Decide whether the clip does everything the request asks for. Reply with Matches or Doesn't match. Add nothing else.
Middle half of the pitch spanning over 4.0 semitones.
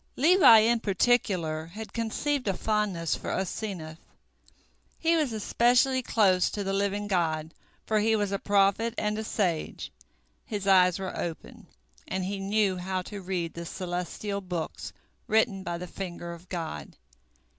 Doesn't match